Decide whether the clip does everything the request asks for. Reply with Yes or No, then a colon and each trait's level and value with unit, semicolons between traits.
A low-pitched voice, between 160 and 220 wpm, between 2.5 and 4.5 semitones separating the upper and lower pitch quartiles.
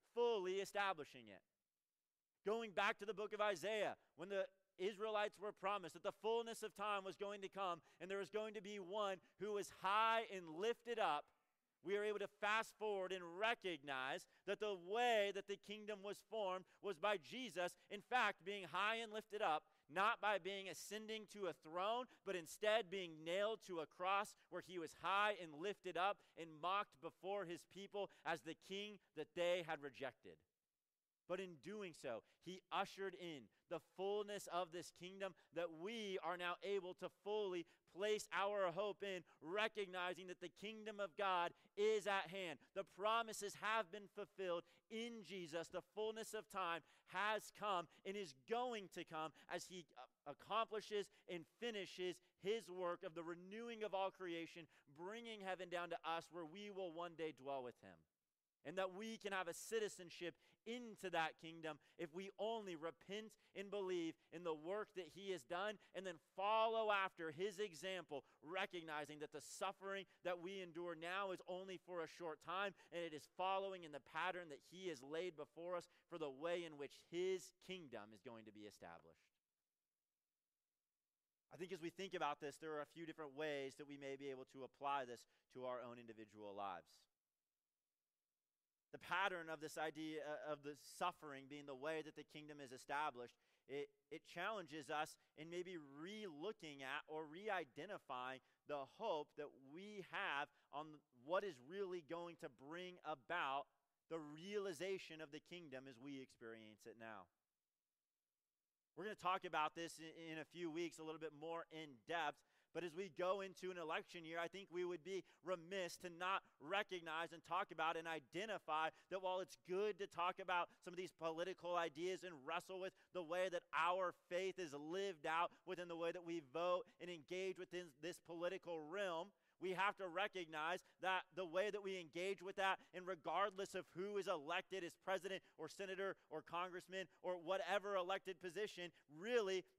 No: medium, 180 Hz; average, 180 wpm; average, 4.0 semitones